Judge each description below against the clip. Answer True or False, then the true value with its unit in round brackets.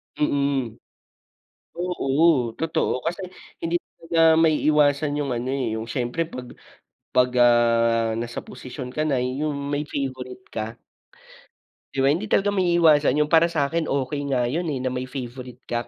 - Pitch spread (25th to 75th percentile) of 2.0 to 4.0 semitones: True (3.7 semitones)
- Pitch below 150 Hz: True (140 Hz)